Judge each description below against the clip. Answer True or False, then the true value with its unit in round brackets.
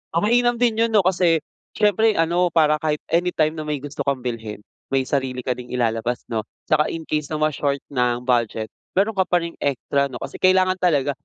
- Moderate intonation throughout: False (6.0 semitones)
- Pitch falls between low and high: True (150 Hz)